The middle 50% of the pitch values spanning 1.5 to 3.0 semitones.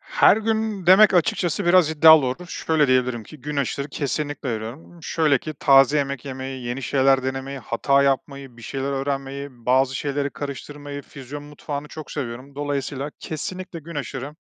Yes: narrow, 2.4 semitones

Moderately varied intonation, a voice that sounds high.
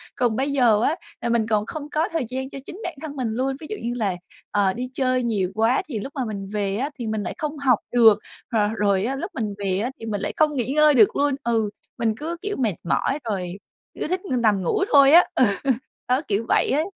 Yes: average, 5.0 semitones; high, 245 Hz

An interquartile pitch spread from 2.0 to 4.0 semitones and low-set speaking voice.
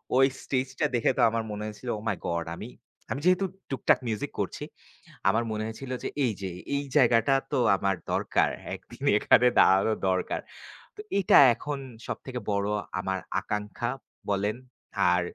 No: average, 4.5 semitones; low, 110 Hz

